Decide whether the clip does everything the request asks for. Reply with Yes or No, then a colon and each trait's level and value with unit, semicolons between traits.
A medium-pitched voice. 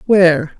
Yes: medium, 170 Hz